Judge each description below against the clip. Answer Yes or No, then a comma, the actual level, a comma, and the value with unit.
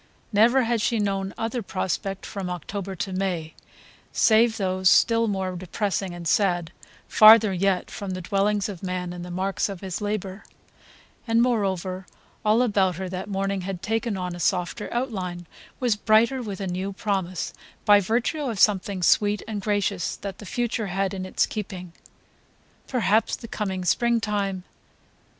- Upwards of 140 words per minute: Yes, average, 160 wpm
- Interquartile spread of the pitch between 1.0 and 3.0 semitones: Yes, average, 2.7 semitones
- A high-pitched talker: Yes, high, 195 Hz